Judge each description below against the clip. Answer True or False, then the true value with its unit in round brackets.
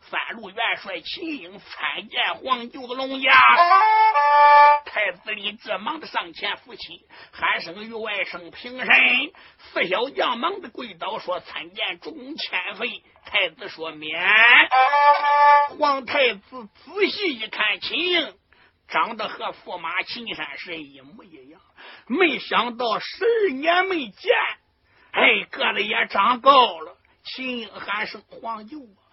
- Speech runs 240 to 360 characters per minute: False (185 characters per minute)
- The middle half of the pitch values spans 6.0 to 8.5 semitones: False (5.6 semitones)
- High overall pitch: True (265 Hz)